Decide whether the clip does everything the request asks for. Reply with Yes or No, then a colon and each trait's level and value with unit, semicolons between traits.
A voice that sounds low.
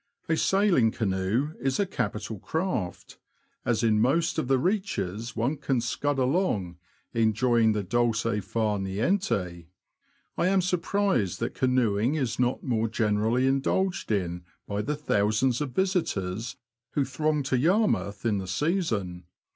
Yes: low, 120 Hz